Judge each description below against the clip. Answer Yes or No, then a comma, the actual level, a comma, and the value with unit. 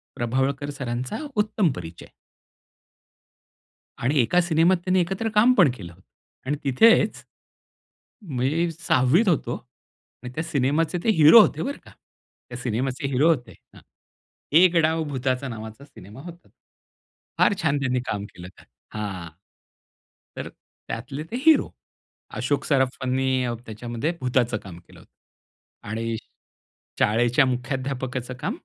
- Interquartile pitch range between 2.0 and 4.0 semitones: No, average, 5.0 semitones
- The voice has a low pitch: Yes, low, 130 Hz